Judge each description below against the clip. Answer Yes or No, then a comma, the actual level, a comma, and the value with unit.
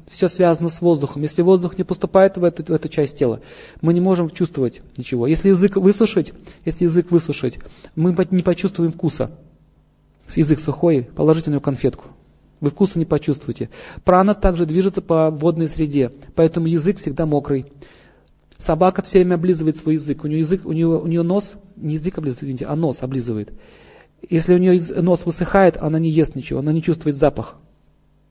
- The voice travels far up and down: No, average, 3.4 semitones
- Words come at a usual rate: No, fast, 175 wpm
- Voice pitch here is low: No, medium, 165 Hz